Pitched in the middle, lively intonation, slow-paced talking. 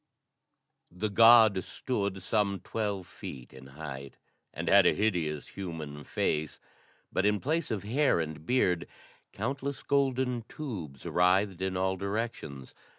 No: low, 100 Hz; wide, 5.9 semitones; slow, 130 wpm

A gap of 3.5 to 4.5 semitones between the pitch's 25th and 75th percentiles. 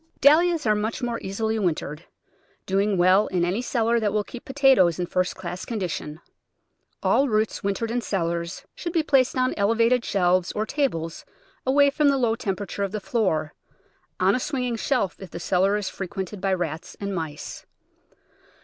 No: average, 5.0 semitones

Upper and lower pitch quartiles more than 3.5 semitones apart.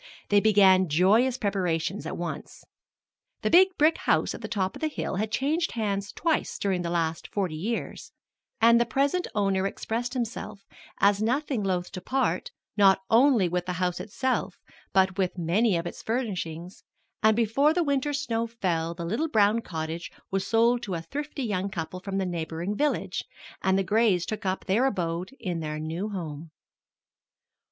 Yes: average, 4.7 semitones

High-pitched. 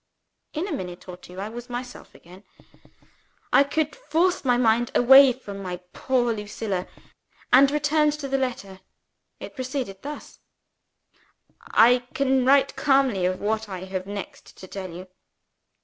Yes: high, 245 Hz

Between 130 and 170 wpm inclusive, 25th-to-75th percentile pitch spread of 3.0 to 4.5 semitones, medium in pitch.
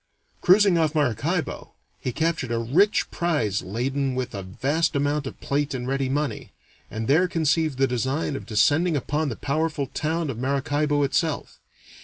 Yes: average, 160 wpm; average, 3.6 semitones; medium, 145 Hz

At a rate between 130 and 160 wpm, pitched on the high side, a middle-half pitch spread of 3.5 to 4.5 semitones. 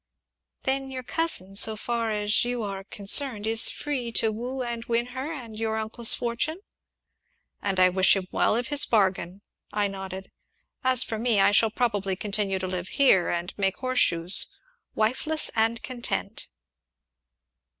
Yes: average, 155 wpm; high, 220 Hz; average, 4.0 semitones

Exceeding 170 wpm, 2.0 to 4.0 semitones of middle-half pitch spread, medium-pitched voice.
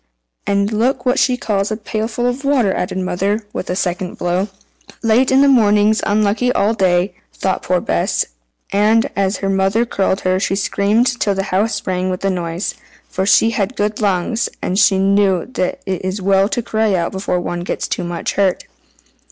No: average, 190 wpm; average, 2.9 semitones; high, 200 Hz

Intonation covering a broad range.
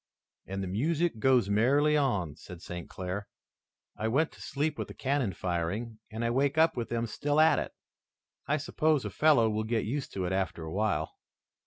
Yes: wide, 6.8 semitones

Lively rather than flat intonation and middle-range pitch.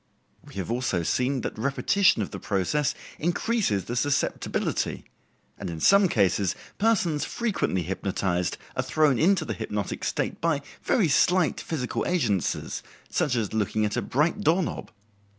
No: wide, 8.8 semitones; low, 130 Hz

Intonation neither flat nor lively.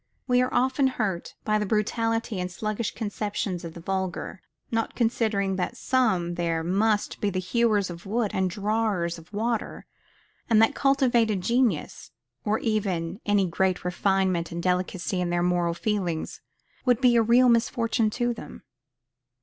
Yes: average, 4.1 semitones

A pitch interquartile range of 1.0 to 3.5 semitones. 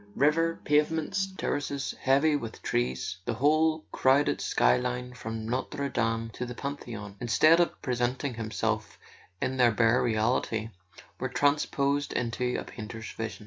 No: average, 4.2 semitones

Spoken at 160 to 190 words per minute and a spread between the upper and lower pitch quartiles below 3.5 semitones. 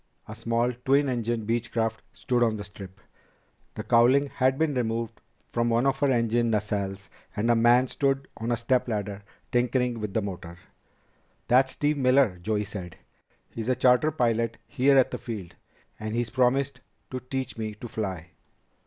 Yes: average, 170 wpm; average, 2.9 semitones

